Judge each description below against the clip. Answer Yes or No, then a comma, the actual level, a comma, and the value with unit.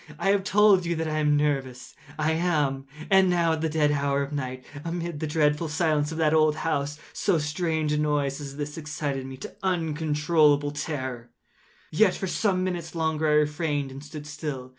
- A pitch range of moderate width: No, narrow, 2.1 semitones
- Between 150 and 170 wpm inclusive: No, average, 200 wpm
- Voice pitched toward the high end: No, medium, 150 Hz